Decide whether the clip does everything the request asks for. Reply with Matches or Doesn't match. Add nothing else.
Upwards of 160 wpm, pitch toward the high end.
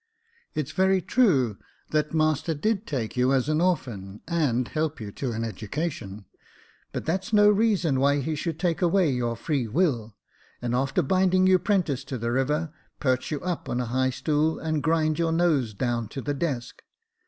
Doesn't match